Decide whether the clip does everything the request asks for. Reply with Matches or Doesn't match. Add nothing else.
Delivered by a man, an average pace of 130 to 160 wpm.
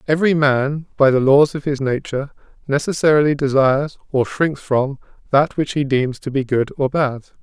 Doesn't match